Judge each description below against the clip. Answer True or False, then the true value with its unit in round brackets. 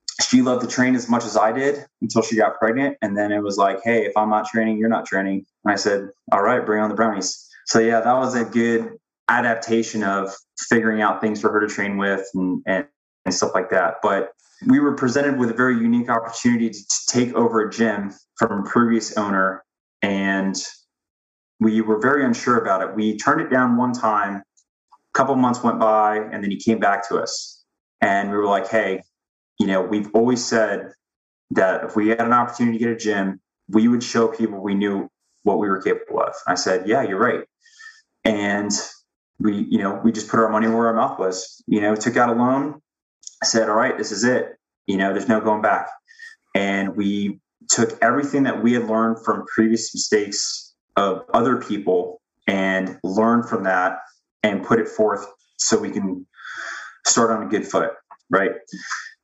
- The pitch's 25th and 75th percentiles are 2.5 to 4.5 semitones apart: True (3.2 semitones)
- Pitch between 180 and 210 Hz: False (110 Hz)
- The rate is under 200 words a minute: False (205 wpm)